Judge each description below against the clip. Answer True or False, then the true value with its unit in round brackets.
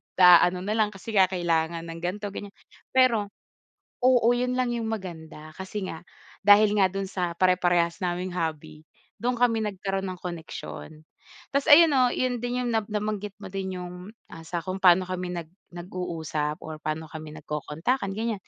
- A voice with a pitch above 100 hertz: True (185 Hz)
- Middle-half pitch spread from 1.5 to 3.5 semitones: False (4.1 semitones)